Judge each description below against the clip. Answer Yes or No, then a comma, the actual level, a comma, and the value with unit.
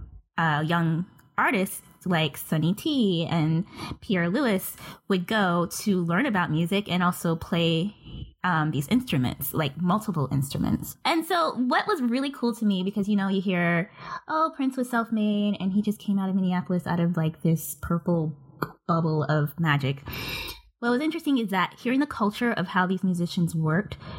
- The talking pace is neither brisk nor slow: Yes, average, 170 wpm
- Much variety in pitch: No, average, 4.1 semitones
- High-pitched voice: No, medium, 180 Hz